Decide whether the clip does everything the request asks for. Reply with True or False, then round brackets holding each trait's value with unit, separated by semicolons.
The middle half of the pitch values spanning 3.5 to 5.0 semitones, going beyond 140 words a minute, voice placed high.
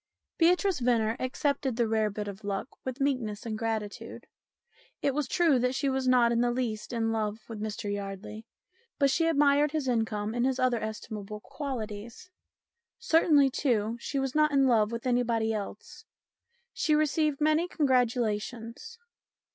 True (4.3 semitones; 155 wpm; 240 Hz)